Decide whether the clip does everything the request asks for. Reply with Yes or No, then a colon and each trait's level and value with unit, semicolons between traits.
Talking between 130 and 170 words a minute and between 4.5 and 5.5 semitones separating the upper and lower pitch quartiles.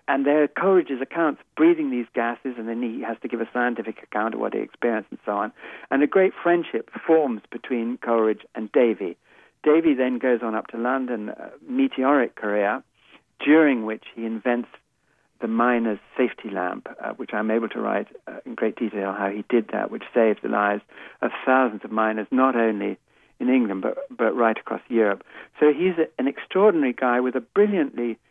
No: average, 195 wpm; average, 4.9 semitones